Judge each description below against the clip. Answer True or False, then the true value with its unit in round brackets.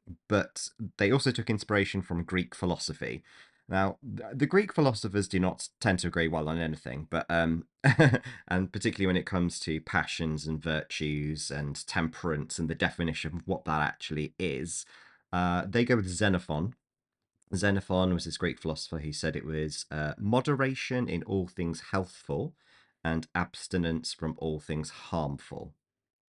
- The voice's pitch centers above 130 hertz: False (90 Hz)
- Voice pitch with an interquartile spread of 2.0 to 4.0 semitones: False (4.4 semitones)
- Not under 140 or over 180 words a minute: True (155 wpm)